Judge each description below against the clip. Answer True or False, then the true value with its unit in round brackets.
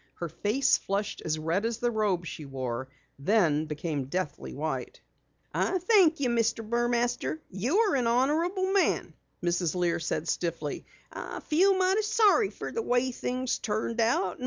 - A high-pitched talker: True (225 Hz)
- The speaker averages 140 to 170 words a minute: True (155 wpm)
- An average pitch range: False (8.9 semitones)